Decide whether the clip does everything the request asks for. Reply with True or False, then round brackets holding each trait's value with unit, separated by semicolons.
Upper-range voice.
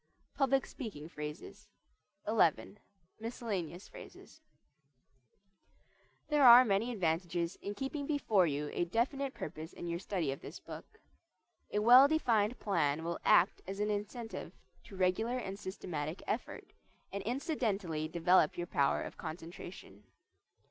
True (195 Hz)